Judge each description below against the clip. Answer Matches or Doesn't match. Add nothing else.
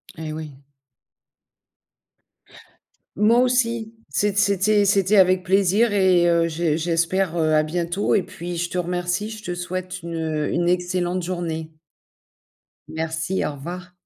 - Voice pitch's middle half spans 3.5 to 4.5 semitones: Doesn't match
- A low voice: Doesn't match